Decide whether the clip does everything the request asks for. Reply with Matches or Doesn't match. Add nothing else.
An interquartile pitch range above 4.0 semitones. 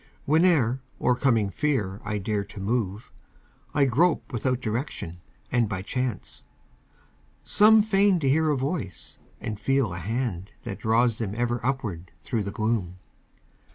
Matches